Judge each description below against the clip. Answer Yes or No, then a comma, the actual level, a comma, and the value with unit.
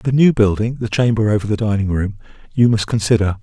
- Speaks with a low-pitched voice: Yes, low, 110 Hz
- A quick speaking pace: Yes, fast, 210 wpm